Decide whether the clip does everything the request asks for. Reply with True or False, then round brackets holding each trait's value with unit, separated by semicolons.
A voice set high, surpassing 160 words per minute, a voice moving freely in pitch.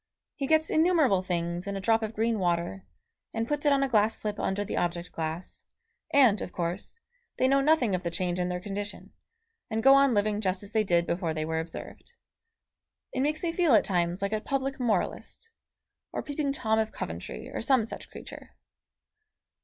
True (215 Hz; 195 wpm; 7.1 semitones)